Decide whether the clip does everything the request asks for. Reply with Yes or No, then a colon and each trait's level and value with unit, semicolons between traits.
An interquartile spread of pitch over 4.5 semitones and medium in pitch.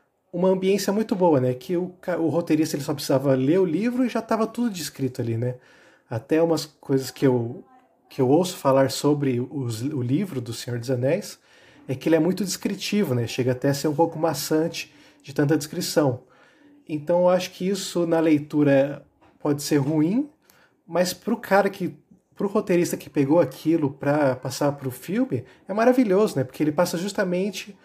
Yes: average, 5.2 semitones; medium, 160 Hz